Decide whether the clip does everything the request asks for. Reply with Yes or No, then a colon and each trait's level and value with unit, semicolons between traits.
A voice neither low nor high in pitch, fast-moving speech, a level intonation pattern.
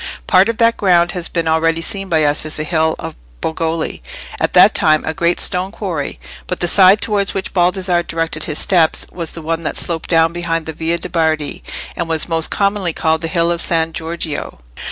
Yes: medium, 165 Hz; fast, 210 wpm; narrow, 2.0 semitones